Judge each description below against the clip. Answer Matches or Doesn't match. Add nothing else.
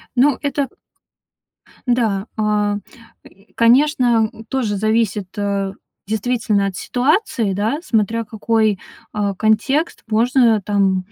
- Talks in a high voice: Matches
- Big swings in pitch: Doesn't match